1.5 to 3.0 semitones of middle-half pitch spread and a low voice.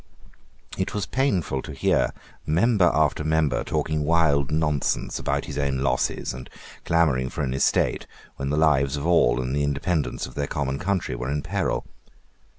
No: average, 3.5 semitones; very low, 75 Hz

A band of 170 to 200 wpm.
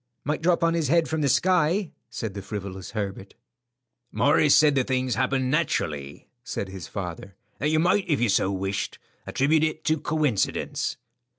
Yes: average, 175 wpm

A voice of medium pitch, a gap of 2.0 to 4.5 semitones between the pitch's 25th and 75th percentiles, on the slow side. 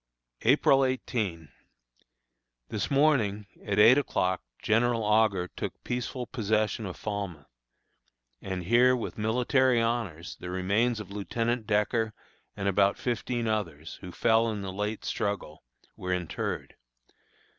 No: low, 110 Hz; average, 3.4 semitones; slow, 125 wpm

